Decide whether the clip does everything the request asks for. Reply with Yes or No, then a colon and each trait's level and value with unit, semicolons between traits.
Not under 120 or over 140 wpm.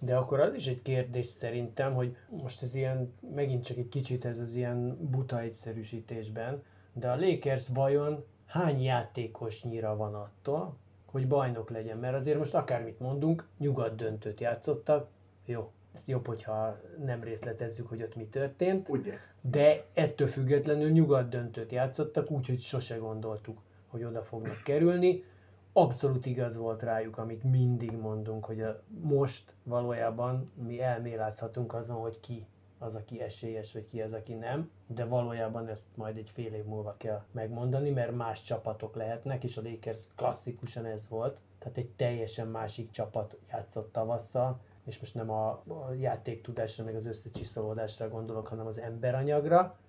No: average, 150 wpm